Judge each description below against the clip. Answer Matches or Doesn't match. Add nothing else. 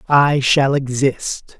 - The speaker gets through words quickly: Doesn't match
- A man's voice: Matches